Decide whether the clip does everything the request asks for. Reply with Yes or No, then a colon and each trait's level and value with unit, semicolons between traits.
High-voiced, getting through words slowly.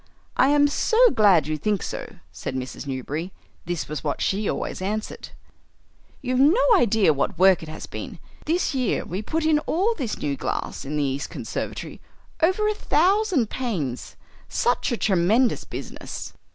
No: high, 215 Hz; average, 165 wpm